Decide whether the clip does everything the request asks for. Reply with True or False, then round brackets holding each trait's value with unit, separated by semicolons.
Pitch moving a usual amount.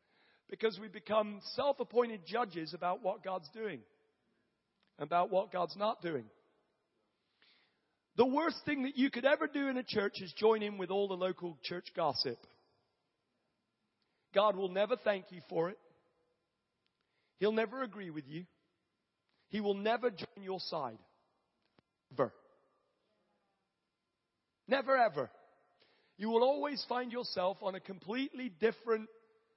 True (4.3 semitones)